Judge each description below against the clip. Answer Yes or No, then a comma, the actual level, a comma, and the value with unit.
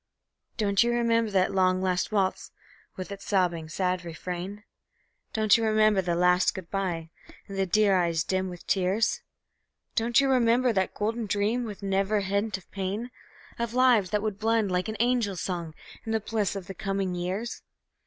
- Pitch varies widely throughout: No, average, 3.2 semitones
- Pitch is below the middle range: No, high, 195 Hz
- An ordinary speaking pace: Yes, average, 180 wpm